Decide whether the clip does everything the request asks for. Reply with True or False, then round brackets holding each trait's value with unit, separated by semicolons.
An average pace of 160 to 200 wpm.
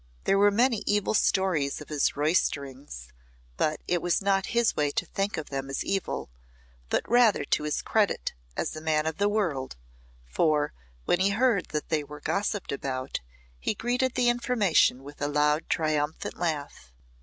True (170 wpm)